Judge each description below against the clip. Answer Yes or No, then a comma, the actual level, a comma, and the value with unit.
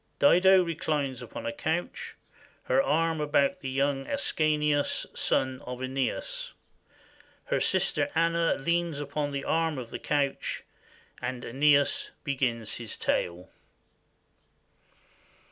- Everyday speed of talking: No, slow, 110 wpm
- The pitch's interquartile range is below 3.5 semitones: No, average, 4.0 semitones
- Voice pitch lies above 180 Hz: No, medium, 145 Hz